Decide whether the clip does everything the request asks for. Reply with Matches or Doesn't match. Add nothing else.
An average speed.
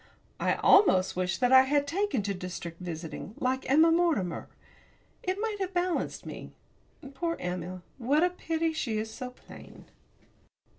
Matches